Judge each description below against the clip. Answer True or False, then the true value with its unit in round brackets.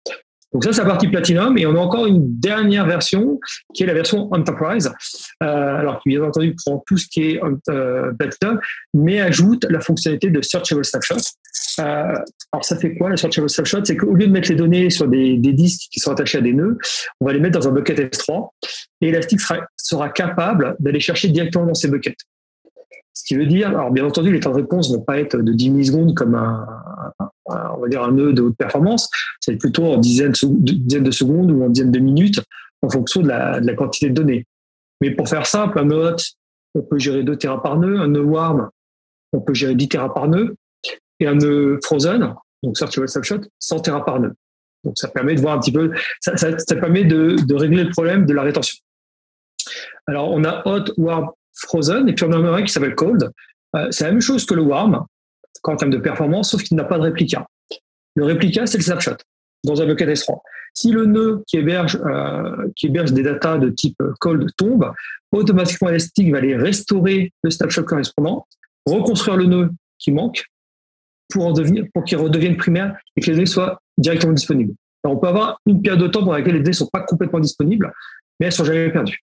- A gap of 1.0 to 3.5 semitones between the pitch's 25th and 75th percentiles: False (4.4 semitones)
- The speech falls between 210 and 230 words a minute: True (220 wpm)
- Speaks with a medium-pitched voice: True (165 Hz)